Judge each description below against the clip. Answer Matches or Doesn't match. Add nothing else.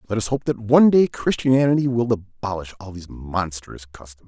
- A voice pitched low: Matches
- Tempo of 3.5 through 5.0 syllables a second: Doesn't match